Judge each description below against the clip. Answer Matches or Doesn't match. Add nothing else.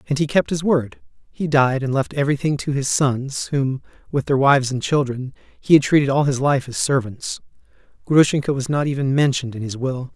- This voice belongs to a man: Matches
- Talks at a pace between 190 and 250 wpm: Matches